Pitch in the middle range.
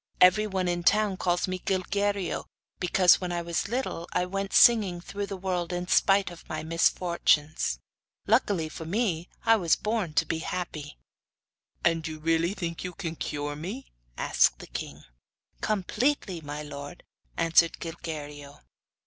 Yes: medium, 175 Hz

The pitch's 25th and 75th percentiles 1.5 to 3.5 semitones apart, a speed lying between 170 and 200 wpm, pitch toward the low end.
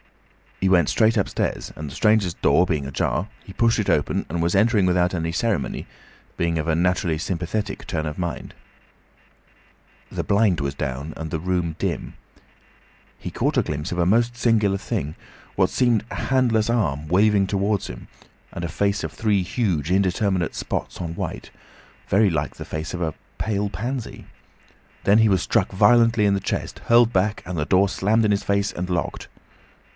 No: average, 4.3 semitones; average, 180 wpm; very low, 95 Hz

